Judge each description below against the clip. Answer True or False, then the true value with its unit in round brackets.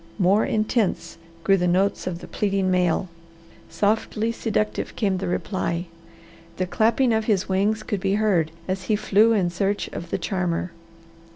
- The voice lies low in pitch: False (195 Hz)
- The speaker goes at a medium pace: True (160 wpm)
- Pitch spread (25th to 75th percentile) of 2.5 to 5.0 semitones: True (2.8 semitones)